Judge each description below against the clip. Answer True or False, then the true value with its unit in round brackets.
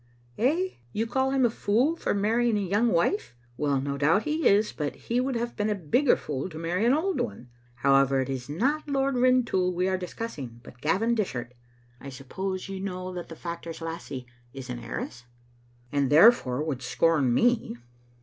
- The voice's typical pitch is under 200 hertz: True (185 Hz)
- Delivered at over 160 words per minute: True (190 wpm)